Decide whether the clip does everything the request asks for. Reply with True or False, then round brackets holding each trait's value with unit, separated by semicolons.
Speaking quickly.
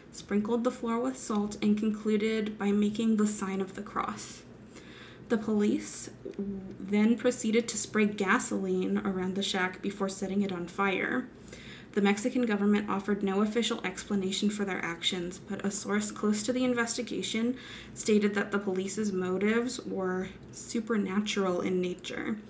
False (145 wpm)